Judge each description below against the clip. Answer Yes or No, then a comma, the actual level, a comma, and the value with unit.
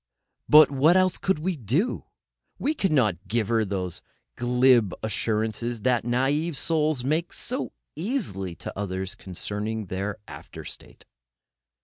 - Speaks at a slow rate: Yes, slow, 130 wpm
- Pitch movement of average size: No, wide, 6.9 semitones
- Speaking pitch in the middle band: No, low, 120 Hz